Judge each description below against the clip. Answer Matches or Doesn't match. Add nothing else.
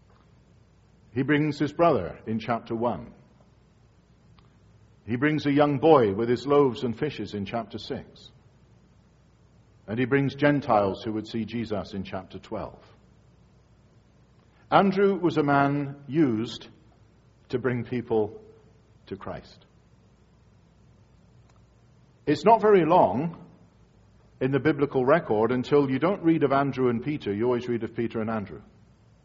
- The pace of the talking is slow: Matches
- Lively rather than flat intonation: Doesn't match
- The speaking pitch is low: Matches